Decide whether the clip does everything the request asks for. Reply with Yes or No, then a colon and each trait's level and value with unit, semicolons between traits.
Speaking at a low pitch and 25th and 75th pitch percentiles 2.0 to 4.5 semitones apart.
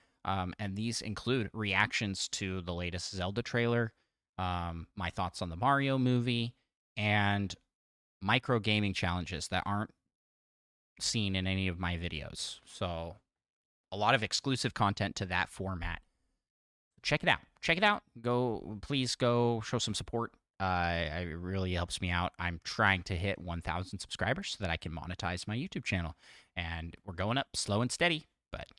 No: low, 100 Hz; average, 4.9 semitones